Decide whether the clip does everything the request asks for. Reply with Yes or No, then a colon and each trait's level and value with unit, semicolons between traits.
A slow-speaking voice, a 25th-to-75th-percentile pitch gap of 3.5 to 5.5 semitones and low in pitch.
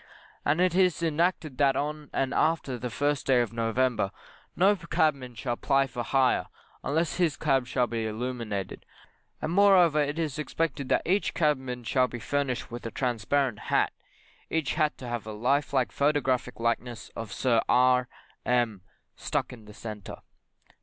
No: average, 165 wpm; average, 4.1 semitones; low, 130 Hz